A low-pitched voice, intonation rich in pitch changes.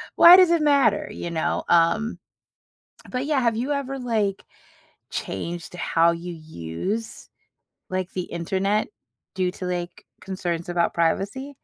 No: high, 190 Hz; wide, 6.3 semitones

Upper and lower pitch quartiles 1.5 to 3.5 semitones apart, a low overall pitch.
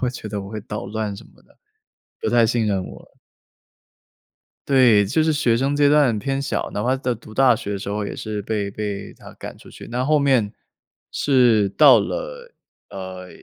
No: average, 4.8 semitones; low, 115 Hz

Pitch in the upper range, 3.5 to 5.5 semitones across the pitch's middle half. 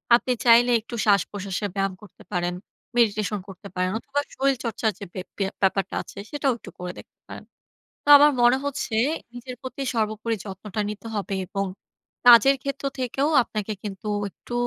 Yes: high, 215 Hz; average, 3.9 semitones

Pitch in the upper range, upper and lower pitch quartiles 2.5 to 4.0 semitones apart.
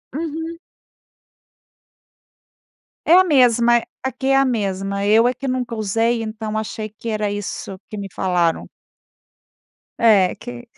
Yes: high, 225 Hz; average, 3.6 semitones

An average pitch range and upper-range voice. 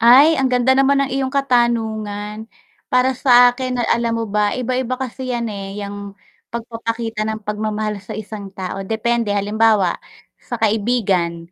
Yes: average, 3.2 semitones; high, 225 Hz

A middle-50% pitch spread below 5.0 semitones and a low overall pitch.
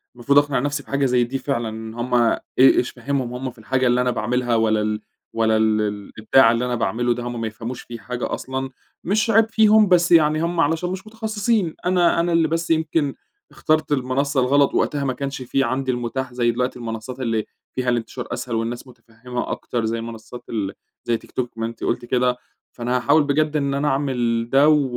Yes: average, 3.7 semitones; low, 125 Hz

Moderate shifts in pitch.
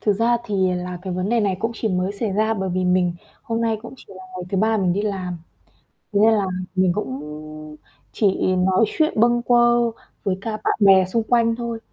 Yes: average, 3.6 semitones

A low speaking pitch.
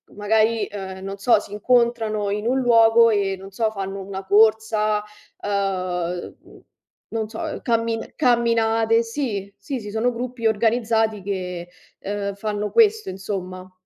No: high, 215 Hz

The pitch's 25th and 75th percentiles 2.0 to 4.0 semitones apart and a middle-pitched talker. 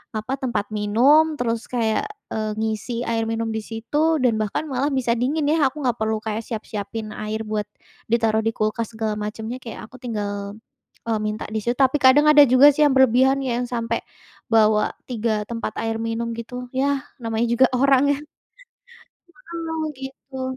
No: average, 3.2 semitones; high, 230 Hz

